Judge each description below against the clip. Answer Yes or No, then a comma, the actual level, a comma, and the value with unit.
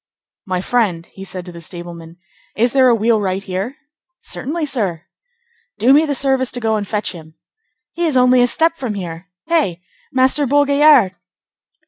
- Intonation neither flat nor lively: No, wide, 6.5 semitones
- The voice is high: Yes, high, 230 Hz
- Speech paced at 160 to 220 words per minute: Yes, average, 165 wpm